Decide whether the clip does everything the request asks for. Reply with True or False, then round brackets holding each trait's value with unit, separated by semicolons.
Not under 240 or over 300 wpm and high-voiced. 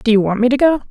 False (400 wpm; 240 Hz)